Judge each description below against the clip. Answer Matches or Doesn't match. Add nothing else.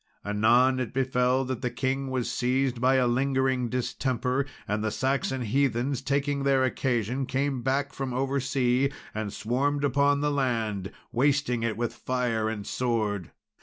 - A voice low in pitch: Matches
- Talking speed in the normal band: Matches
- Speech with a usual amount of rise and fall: Doesn't match